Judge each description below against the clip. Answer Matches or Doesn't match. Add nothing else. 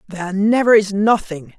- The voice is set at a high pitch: Matches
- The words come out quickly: Doesn't match